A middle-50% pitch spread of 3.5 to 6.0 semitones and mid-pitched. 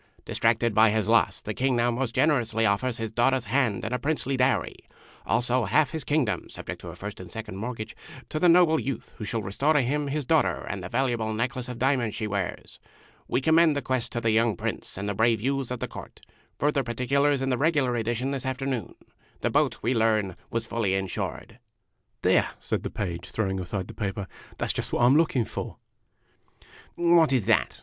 No: average, 3.8 semitones; low, 120 Hz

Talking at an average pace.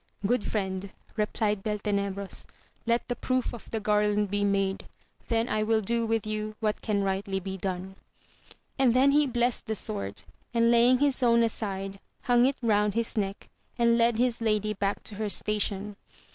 Yes: average, 170 wpm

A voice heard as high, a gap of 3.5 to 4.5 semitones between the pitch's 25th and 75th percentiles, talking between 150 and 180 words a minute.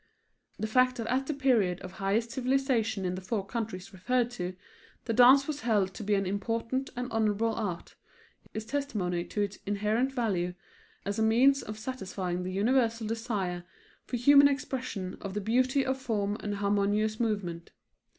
Yes: high, 220 Hz; average, 4.2 semitones; average, 170 wpm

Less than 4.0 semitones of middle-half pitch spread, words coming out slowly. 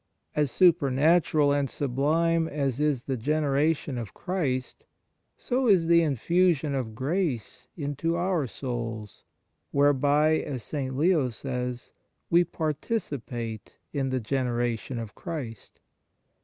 No: average, 4.4 semitones; slow, 115 wpm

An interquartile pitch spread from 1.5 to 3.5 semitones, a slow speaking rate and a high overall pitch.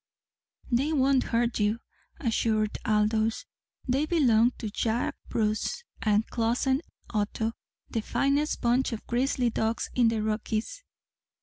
Yes: average, 3.1 semitones; slow, 120 wpm; high, 230 Hz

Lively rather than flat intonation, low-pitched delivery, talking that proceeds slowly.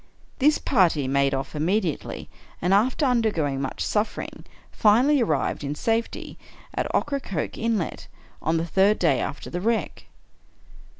No: wide, 7.3 semitones; high, 190 Hz; slow, 130 wpm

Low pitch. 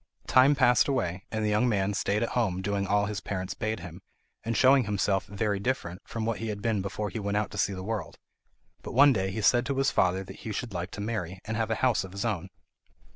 Yes: low, 105 Hz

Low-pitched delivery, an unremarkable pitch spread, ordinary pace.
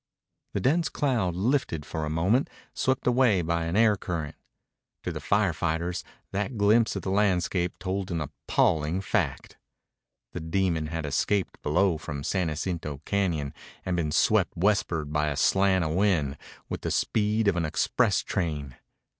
Yes: very low, 90 Hz; average, 4.3 semitones; average, 160 wpm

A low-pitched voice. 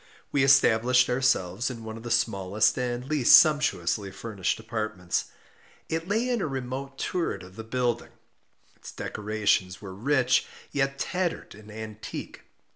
Yes: low, 120 Hz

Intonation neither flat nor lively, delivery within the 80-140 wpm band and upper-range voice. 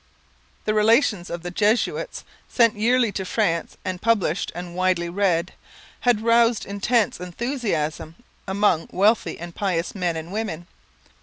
Yes: average, 4.5 semitones; slow, 135 wpm; high, 195 Hz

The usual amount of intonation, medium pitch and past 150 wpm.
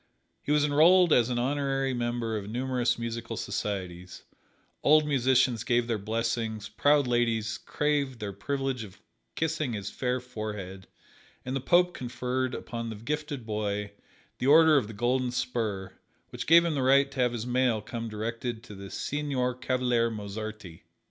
No: average, 3.7 semitones; low, 120 Hz; average, 160 wpm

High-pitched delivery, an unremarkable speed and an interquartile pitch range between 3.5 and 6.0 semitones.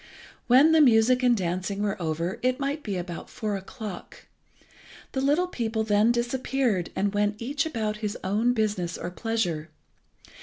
Yes: high, 220 Hz; average, 155 wpm; average, 4.4 semitones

